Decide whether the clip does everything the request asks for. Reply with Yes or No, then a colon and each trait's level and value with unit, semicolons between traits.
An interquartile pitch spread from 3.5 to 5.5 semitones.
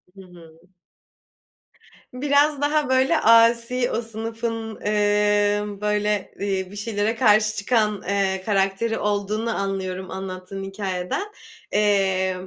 No: average, 2.8 semitones